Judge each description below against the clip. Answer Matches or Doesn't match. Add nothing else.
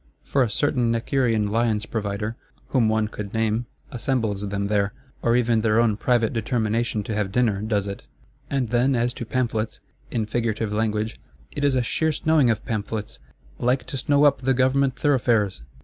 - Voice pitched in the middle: Doesn't match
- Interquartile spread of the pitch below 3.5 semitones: Matches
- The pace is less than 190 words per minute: Matches